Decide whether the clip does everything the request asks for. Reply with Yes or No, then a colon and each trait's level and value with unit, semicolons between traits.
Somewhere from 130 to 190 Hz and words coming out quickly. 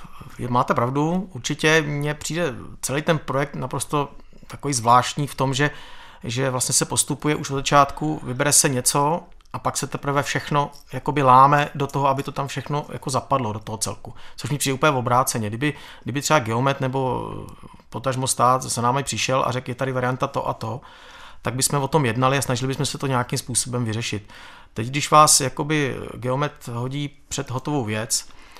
Yes: low, 135 Hz; fast, 185 wpm